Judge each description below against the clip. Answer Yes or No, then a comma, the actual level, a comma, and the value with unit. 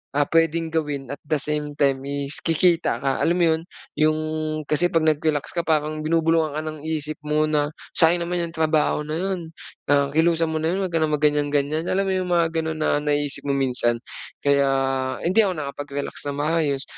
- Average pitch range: No, narrow, 2.2 semitones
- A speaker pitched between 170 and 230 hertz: No, medium, 155 Hz